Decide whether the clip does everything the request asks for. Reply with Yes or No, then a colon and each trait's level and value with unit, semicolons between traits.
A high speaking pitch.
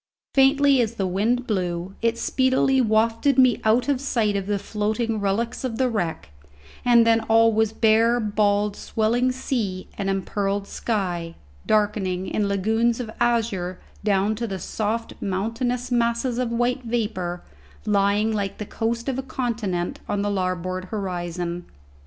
Yes: high, 215 Hz